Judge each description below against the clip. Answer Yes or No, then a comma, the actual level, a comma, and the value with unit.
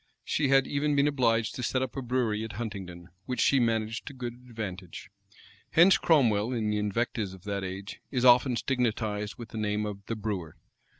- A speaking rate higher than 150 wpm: Yes, average, 190 wpm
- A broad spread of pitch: No, average, 3.4 semitones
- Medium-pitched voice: No, low, 115 Hz